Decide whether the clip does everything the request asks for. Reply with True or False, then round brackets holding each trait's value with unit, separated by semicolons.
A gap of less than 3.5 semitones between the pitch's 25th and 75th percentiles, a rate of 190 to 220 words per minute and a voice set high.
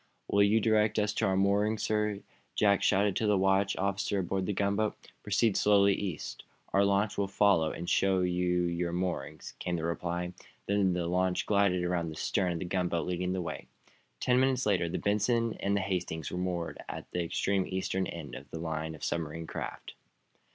False (2.6 semitones; 195 wpm; 95 Hz)